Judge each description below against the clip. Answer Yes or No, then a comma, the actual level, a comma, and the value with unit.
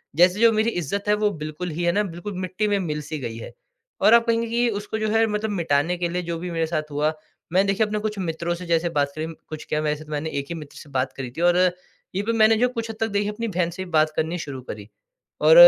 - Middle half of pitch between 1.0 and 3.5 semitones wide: No, average, 5.2 semitones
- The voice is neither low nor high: Yes, medium, 175 Hz